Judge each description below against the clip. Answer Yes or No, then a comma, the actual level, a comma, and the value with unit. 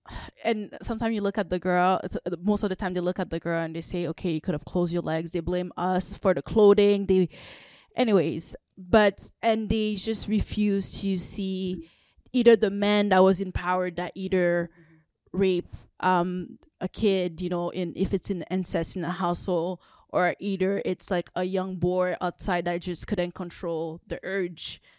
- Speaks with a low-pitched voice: No, medium, 185 Hz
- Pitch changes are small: Yes, narrow, 2.2 semitones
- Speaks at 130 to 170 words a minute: No, average, 190 wpm